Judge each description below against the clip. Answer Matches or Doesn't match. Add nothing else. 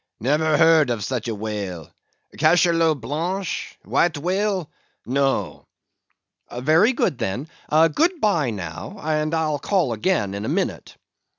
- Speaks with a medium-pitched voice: Matches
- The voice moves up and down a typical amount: Doesn't match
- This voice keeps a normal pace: Doesn't match